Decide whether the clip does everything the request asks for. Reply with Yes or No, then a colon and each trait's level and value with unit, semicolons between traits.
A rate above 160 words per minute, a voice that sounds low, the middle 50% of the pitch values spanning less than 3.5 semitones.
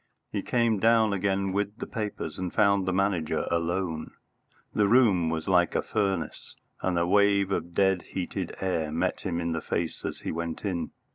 Yes: average, 185 wpm; very low, 95 Hz; average, 3.0 semitones